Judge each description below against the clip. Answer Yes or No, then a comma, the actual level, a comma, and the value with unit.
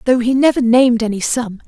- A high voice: Yes, high, 240 Hz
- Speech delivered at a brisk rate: Yes, fast, 215 wpm